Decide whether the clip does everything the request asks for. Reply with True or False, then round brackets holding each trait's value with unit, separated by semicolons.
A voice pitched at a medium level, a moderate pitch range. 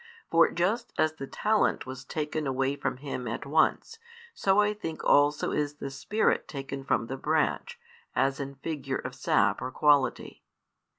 True (145 Hz; 3.5 semitones)